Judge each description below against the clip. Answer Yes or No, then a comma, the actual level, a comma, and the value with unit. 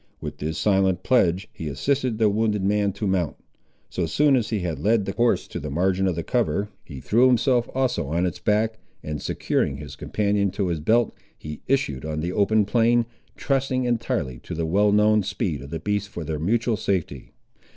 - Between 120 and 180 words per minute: No, average, 200 wpm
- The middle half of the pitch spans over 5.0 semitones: Yes, wide, 5.4 semitones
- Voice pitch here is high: No, low, 100 Hz